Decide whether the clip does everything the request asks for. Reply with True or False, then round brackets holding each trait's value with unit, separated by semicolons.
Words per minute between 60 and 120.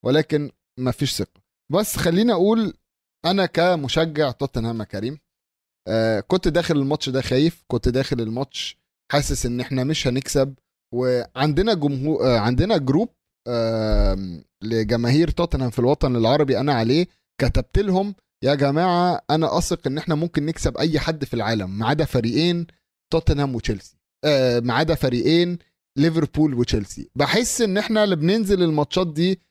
False (130 wpm)